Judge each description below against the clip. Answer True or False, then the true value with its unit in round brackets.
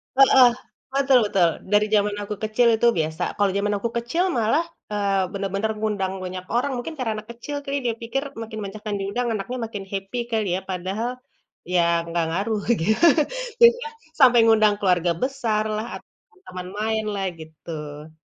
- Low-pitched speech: False (215 Hz)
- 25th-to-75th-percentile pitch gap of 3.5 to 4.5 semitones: True (3.8 semitones)